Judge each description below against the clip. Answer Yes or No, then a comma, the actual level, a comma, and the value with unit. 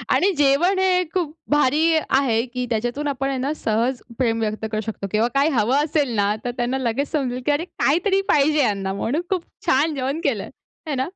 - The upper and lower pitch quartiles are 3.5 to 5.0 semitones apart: Yes, average, 4.1 semitones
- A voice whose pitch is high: Yes, very high, 270 Hz